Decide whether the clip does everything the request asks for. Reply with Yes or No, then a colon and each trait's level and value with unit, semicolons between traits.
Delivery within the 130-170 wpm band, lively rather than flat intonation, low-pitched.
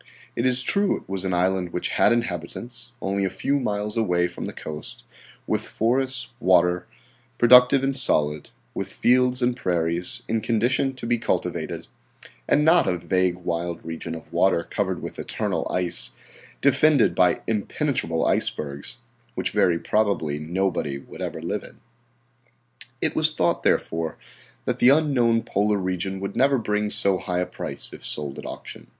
Yes: average, 160 wpm; wide, 6.0 semitones; low, 100 Hz